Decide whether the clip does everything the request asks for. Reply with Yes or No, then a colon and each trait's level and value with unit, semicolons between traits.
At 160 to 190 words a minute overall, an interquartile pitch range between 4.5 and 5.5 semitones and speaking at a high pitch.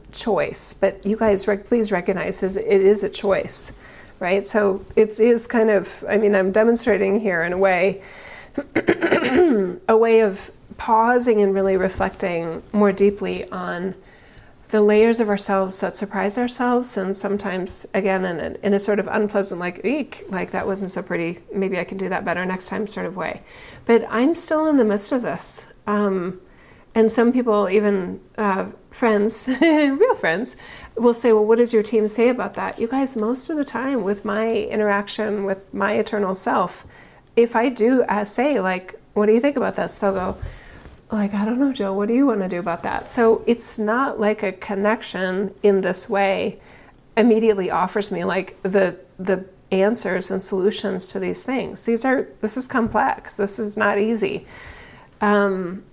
No: average, 180 wpm; average, 2.7 semitones; high, 205 Hz